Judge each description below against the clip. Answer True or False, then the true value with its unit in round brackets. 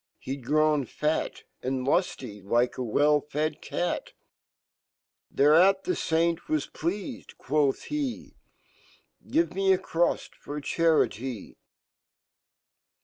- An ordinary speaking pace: False (80 wpm)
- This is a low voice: False (155 Hz)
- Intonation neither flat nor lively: True (4.5 semitones)